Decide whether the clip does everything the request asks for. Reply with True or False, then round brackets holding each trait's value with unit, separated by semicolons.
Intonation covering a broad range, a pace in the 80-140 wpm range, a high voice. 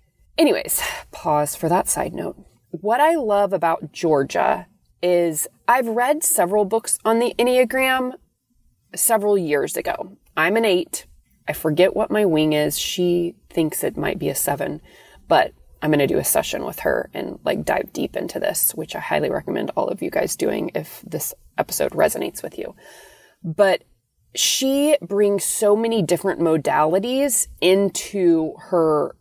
False (5.8 semitones; 160 wpm; 195 Hz)